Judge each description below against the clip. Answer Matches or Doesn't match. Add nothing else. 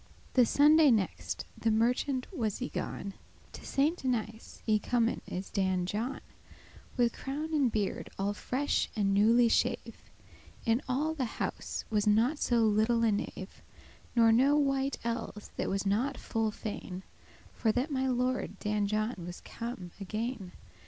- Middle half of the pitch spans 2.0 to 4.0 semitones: Matches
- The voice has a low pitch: Doesn't match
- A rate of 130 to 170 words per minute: Matches